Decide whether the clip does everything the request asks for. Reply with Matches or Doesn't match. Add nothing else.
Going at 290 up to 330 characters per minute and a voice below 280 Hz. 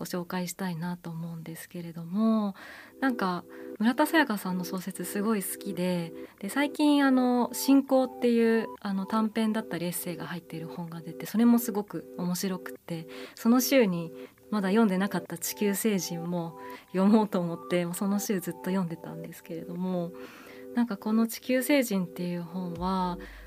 Doesn't match